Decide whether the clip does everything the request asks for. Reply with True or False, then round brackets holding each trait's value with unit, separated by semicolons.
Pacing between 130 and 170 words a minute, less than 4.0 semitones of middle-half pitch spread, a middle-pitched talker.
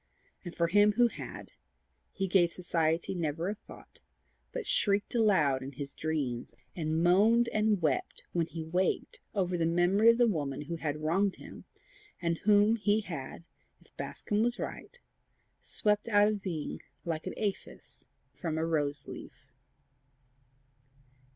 False (150 wpm; 4.6 semitones; 175 Hz)